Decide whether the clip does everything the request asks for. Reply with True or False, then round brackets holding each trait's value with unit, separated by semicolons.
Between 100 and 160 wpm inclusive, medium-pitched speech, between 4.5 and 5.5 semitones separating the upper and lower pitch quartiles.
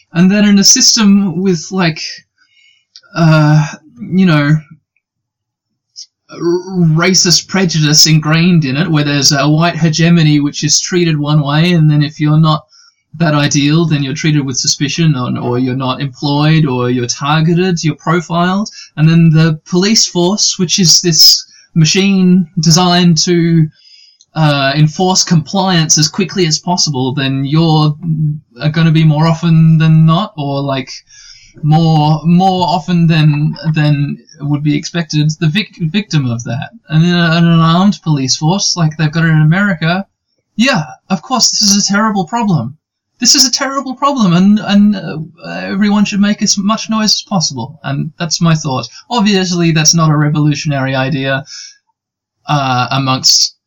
False (155 wpm; 160 Hz; 3.8 semitones)